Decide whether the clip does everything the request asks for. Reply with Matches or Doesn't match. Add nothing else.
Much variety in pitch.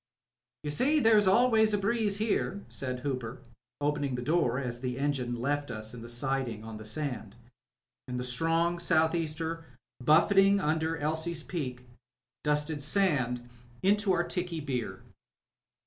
Matches